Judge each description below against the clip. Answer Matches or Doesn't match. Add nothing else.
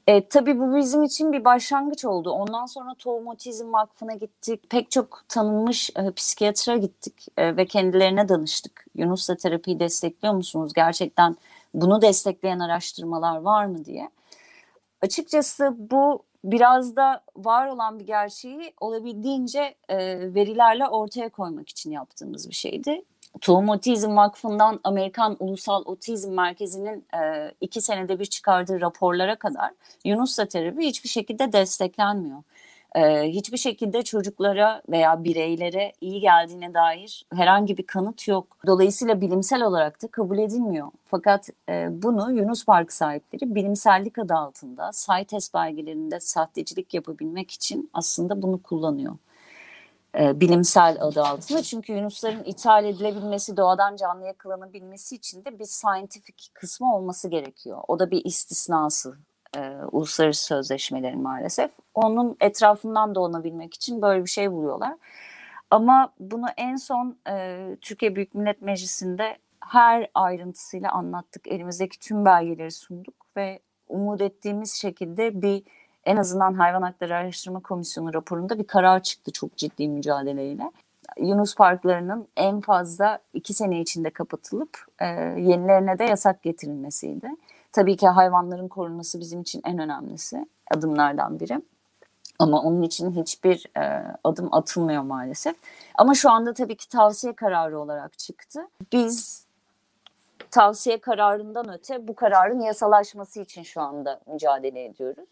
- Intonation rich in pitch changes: Doesn't match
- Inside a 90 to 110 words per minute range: Doesn't match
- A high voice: Matches